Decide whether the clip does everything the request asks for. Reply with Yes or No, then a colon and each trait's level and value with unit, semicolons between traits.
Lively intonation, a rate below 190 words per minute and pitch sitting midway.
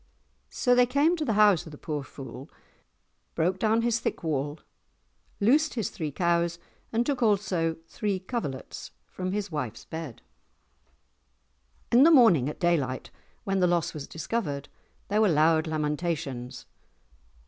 Yes: wide, 6.6 semitones; average, 145 wpm; medium, 175 Hz